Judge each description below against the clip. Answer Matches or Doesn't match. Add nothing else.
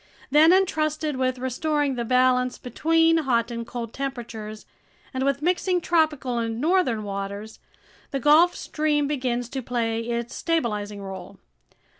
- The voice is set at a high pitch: Matches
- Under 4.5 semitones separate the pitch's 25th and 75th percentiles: Doesn't match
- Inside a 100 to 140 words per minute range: Matches